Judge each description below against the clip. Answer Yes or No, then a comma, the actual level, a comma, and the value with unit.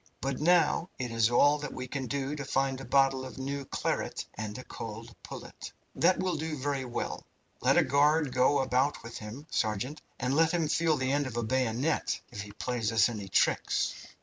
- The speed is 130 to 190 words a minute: No, average, 200 wpm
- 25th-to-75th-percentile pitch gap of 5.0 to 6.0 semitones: No, average, 3.4 semitones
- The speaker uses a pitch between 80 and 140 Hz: Yes, low, 135 Hz